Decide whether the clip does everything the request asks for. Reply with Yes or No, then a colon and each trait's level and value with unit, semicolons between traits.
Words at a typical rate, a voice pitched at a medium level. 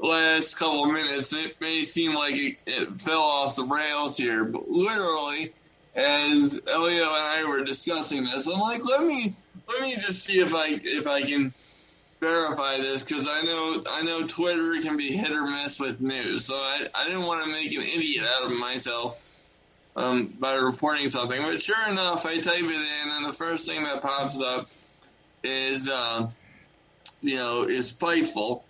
Yes: average, 185 wpm; medium, 155 Hz